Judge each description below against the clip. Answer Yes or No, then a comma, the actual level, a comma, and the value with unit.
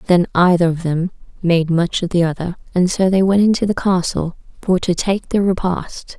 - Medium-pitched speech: Yes, medium, 180 Hz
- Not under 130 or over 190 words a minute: No, fast, 205 wpm